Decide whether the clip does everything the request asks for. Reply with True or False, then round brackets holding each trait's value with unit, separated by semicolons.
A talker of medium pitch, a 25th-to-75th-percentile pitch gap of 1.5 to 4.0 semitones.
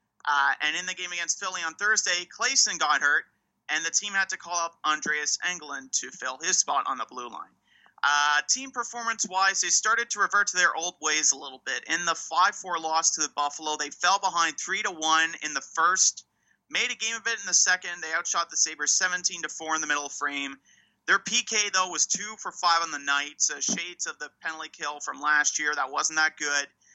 False (170 Hz; 5.0 semitones)